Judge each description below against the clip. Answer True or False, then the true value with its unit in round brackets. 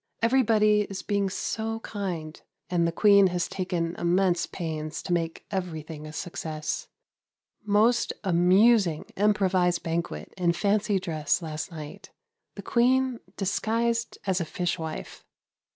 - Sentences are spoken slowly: True (125 wpm)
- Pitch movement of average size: True (3.9 semitones)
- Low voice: False (185 Hz)